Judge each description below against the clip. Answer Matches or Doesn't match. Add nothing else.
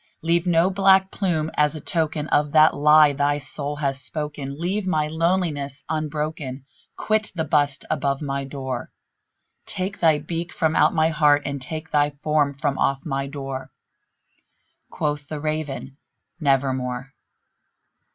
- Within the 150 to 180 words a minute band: Doesn't match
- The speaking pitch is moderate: Matches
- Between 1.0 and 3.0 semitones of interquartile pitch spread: Matches